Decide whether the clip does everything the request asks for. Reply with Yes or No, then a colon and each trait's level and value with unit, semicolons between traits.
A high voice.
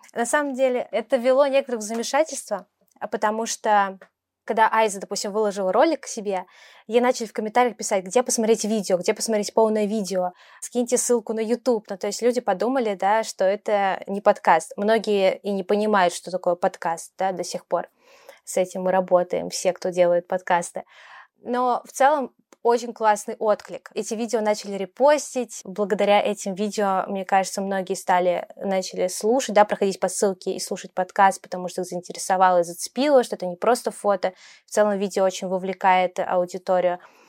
Yes: high, 205 Hz